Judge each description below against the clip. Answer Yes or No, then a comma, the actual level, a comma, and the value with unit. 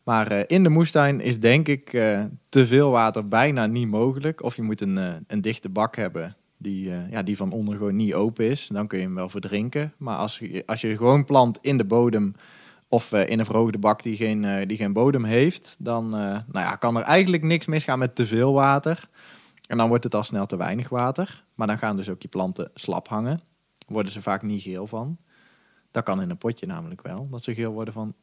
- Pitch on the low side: Yes, low, 115 Hz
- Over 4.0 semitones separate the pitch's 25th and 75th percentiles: Yes, average, 4.4 semitones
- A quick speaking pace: Yes, fast, 225 wpm